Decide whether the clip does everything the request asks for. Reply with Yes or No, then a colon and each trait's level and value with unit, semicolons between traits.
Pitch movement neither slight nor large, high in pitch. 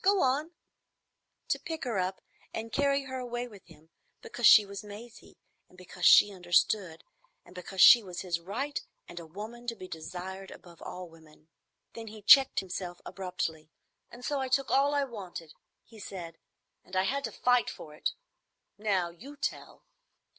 No: wide, 5.7 semitones; high, 200 Hz